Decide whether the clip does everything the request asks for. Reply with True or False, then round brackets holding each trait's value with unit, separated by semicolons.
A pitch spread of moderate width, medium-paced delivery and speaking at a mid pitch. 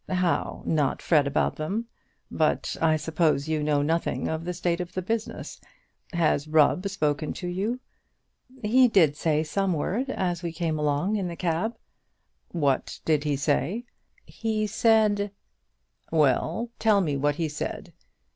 True (4.8 semitones; 155 wpm; 165 Hz)